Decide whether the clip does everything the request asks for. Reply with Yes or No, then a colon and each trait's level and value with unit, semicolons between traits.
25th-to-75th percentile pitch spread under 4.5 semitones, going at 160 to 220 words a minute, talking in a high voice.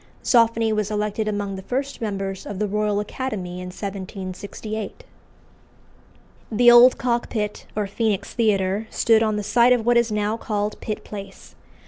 No: narrow, 2.4 semitones; average, 150 wpm; high, 210 Hz